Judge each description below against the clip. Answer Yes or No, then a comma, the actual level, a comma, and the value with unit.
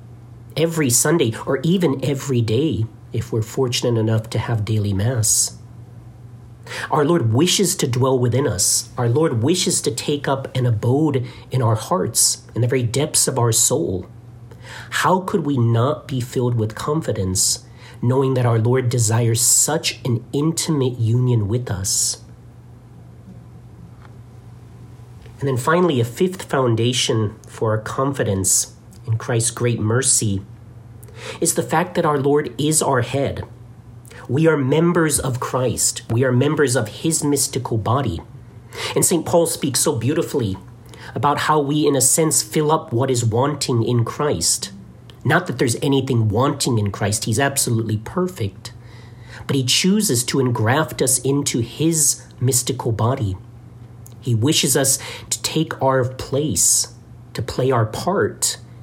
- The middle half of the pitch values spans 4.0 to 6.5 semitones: No, average, 3.1 semitones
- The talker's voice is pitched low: Yes, low, 120 Hz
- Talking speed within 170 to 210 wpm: No, average, 145 wpm